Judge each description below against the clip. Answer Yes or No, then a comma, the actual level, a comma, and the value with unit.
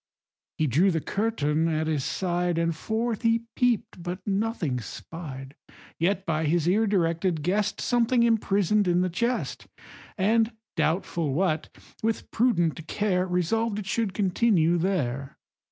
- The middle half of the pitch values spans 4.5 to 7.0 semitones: Yes, average, 5.1 semitones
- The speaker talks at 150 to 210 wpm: No, slow, 135 wpm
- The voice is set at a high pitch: No, medium, 180 Hz